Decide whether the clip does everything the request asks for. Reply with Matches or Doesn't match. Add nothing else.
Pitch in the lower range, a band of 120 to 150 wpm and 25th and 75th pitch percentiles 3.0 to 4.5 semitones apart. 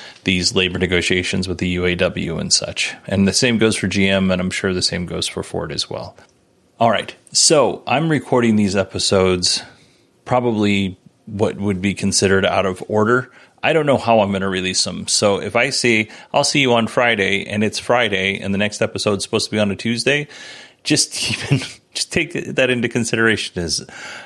Doesn't match